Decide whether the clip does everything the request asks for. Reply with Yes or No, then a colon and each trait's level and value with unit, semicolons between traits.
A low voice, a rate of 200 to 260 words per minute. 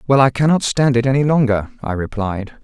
Yes: low, 125 Hz; fast, 205 wpm